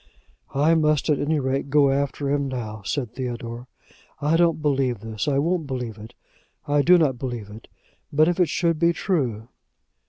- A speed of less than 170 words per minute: No, average, 180 wpm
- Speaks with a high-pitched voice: No, medium, 140 Hz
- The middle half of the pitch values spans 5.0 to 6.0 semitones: No, average, 4.1 semitones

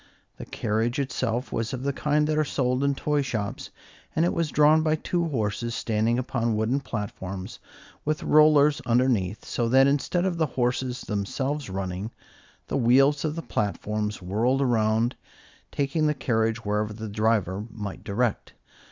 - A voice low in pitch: Yes, low, 125 Hz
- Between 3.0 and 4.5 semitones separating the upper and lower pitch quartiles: No, average, 4.9 semitones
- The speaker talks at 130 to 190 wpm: Yes, average, 160 wpm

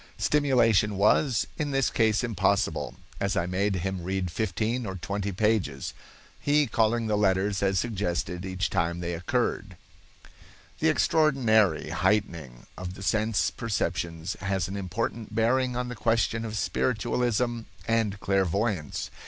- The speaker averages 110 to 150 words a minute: Yes, slow, 135 wpm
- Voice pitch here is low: Yes, low, 105 Hz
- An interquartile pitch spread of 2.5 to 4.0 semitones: Yes, average, 3.5 semitones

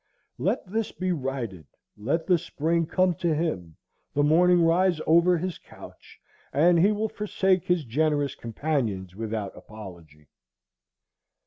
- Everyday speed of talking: No, slow, 130 wpm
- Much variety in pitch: Yes, wide, 7.9 semitones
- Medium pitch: Yes, medium, 160 Hz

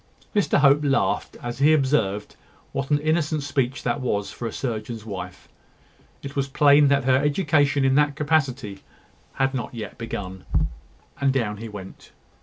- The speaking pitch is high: No, low, 135 Hz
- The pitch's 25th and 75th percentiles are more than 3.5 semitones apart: Yes, average, 3.9 semitones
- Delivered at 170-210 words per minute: No, average, 155 wpm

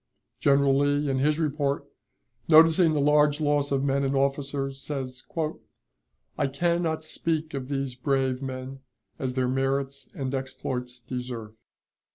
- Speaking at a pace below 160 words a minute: Yes, average, 140 wpm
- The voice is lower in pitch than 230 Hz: Yes, medium, 140 Hz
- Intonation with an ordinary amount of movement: No, narrow, 1.9 semitones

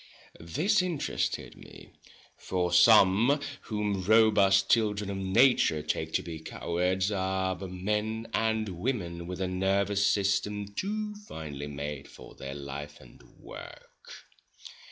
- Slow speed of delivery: Yes, slow, 125 wpm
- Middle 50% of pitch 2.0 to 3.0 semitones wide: No, average, 3.8 semitones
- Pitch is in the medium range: No, very low, 95 Hz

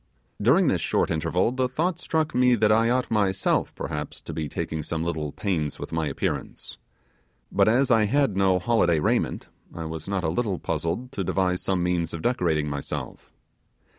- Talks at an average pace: Yes, average, 180 wpm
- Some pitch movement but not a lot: No, wide, 6.5 semitones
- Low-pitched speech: Yes, very low, 95 Hz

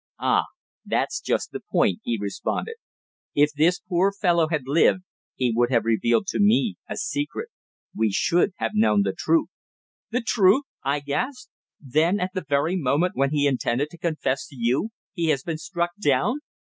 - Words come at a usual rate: Yes, average, 170 wpm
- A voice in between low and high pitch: Yes, medium, 160 Hz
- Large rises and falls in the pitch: Yes, wide, 5.9 semitones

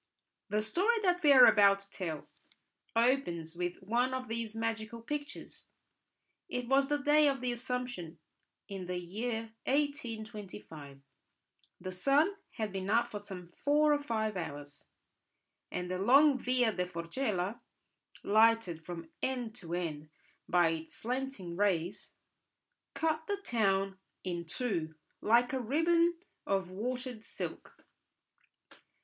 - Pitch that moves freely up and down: Yes, wide, 6.2 semitones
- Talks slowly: Yes, slow, 130 wpm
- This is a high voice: Yes, high, 220 Hz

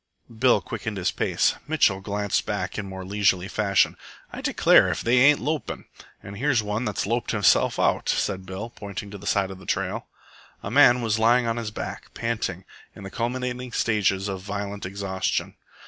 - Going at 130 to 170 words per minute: No, average, 180 wpm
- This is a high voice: No, low, 105 Hz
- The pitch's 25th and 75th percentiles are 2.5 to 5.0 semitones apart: Yes, average, 3.3 semitones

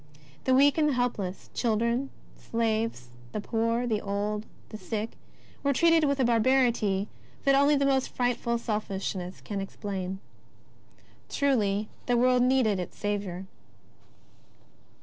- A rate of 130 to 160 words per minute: Yes, slow, 135 wpm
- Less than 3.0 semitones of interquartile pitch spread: No, average, 4.0 semitones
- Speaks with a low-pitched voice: No, high, 230 Hz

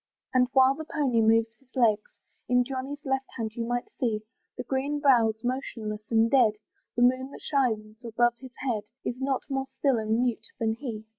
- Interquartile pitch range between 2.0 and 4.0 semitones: Yes, average, 3.1 semitones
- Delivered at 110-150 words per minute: No, average, 190 wpm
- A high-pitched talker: Yes, high, 245 Hz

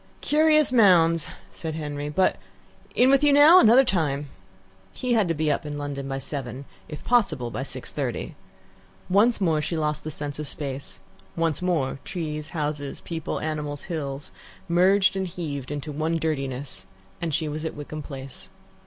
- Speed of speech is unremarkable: Yes, average, 165 wpm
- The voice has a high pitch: No, medium, 155 Hz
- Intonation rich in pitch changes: No, average, 4.0 semitones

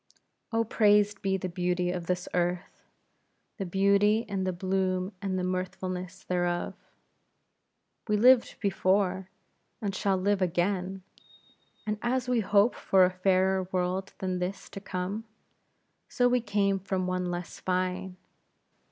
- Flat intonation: Yes, narrow, 1.8 semitones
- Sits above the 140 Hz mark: Yes, high, 190 Hz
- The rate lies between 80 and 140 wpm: Yes, slow, 135 wpm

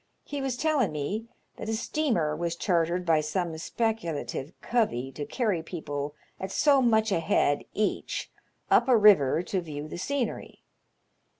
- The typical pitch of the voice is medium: Yes, medium, 180 Hz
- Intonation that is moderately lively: No, wide, 6.9 semitones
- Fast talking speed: No, average, 155 wpm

